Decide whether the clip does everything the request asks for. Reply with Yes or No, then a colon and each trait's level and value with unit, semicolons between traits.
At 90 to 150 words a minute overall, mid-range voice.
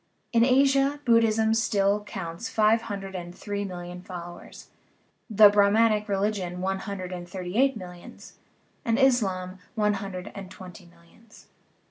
No: average, 140 wpm; high, 200 Hz